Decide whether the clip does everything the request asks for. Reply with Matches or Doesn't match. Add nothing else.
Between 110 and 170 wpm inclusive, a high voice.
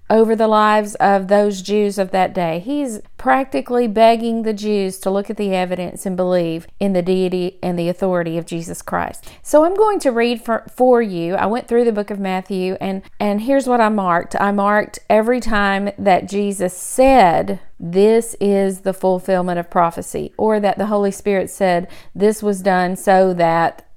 Doesn't match